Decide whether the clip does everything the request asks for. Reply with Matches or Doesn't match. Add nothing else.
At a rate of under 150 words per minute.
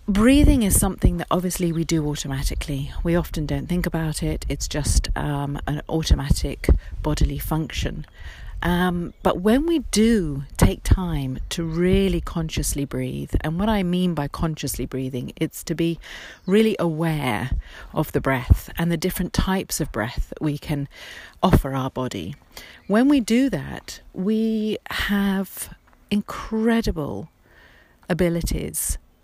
Matches